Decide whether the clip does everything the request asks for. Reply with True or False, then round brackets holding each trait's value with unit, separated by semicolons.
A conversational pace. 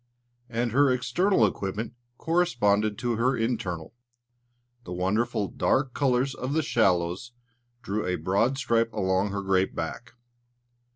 False (125 wpm)